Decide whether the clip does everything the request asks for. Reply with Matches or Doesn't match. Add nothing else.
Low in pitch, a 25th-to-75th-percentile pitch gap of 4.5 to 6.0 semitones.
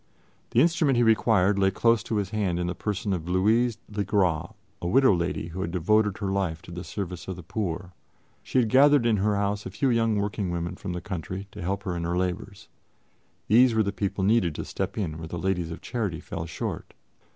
Doesn't match